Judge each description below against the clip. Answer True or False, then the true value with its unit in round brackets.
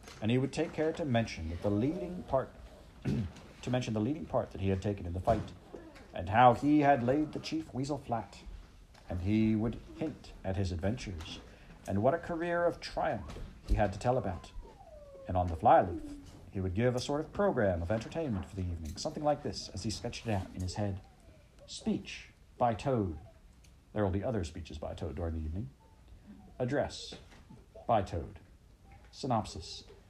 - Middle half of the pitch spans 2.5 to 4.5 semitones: False (5.0 semitones)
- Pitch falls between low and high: False (105 Hz)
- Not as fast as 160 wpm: False (185 wpm)